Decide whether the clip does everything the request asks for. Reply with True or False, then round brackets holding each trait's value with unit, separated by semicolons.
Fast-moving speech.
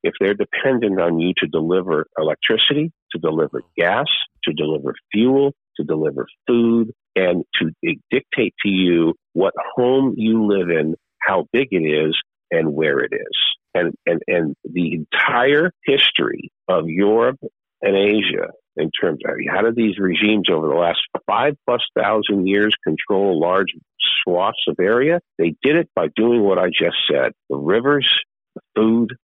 False (160 wpm)